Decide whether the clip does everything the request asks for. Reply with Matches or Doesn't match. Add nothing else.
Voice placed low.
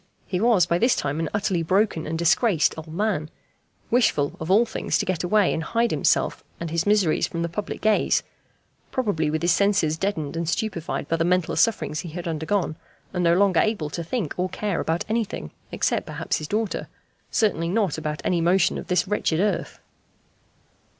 Doesn't match